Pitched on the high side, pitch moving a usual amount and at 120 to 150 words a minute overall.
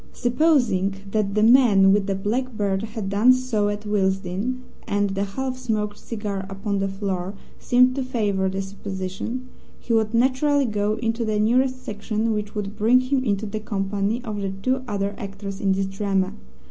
No: high, 210 Hz; average, 3.5 semitones; average, 175 wpm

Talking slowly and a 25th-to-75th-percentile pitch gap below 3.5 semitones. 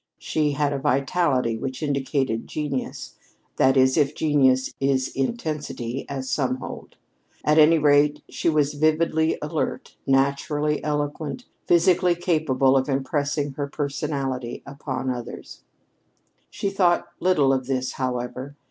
Yes: slow, 125 wpm; narrow, 2.5 semitones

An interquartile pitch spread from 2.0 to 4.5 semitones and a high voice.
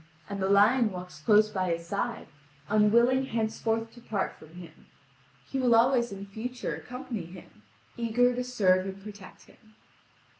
Yes: average, 3.8 semitones; high, 215 Hz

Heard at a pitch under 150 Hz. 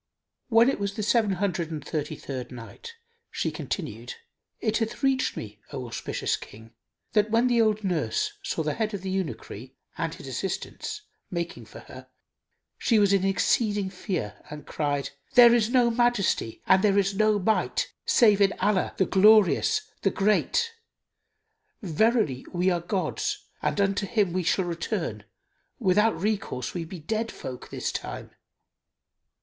No: high, 200 Hz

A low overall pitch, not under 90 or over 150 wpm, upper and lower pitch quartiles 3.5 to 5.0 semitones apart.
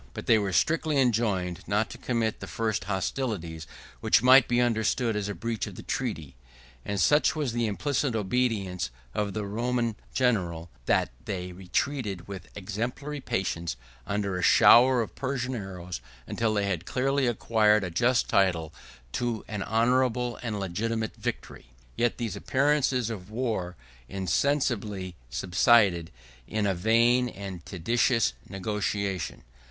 Yes: low, 110 Hz; average, 140 wpm; average, 4.3 semitones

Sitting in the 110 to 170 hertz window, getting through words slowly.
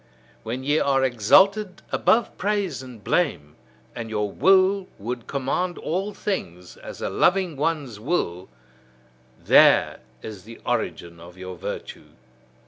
Yes: low, 135 Hz; slow, 130 wpm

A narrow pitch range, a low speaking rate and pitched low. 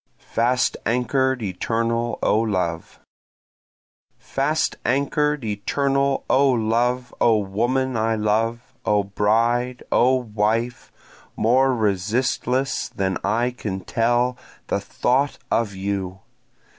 No: average, 3.3 semitones; slow, 100 wpm; low, 115 Hz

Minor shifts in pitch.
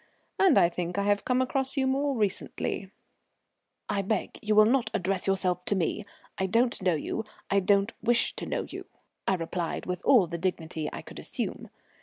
No: average, 4.3 semitones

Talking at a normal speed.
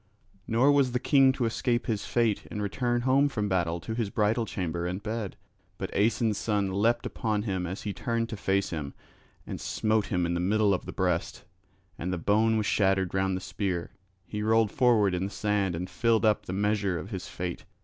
No: fast, 210 wpm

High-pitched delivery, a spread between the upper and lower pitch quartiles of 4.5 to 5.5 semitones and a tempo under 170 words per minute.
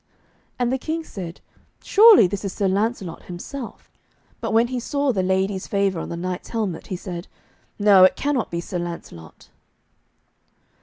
Yes: high, 195 Hz; average, 5.0 semitones; average, 160 wpm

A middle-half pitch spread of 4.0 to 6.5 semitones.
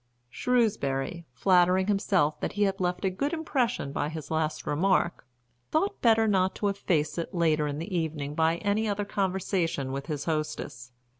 Yes: average, 4.8 semitones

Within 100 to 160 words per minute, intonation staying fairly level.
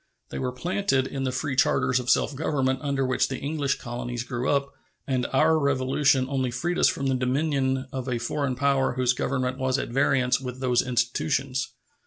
No: average, 190 wpm; narrow, 1.5 semitones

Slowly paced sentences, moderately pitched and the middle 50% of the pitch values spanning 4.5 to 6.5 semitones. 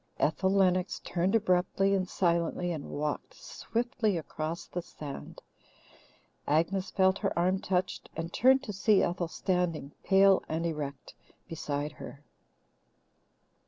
No: slow, 125 wpm; medium, 180 Hz; average, 3.0 semitones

